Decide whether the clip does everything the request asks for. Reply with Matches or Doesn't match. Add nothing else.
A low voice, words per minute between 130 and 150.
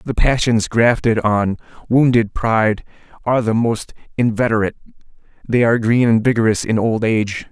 Matches